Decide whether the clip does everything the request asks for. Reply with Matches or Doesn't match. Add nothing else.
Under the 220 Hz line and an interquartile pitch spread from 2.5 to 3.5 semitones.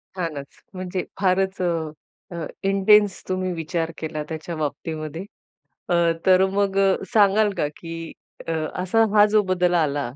Matches